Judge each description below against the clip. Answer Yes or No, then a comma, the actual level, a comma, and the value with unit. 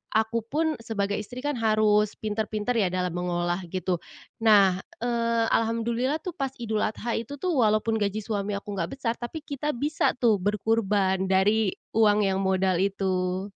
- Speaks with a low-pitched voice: No, high, 215 Hz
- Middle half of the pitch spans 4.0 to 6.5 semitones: No, average, 3.3 semitones